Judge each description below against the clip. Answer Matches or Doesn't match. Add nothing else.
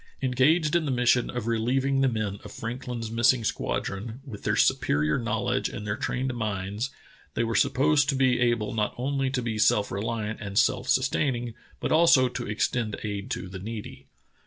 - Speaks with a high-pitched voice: Doesn't match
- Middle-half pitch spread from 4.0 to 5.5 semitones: Doesn't match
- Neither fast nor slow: Matches